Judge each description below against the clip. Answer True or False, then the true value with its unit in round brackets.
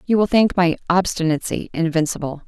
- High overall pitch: False (175 Hz)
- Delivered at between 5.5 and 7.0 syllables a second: True (5.6 syllables/s)